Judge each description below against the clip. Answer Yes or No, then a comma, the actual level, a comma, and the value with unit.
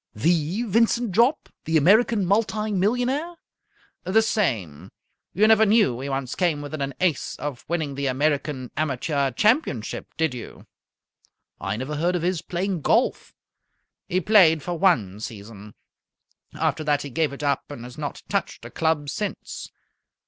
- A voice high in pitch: No, medium, 160 Hz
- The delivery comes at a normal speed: Yes, average, 150 wpm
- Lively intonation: Yes, wide, 6.6 semitones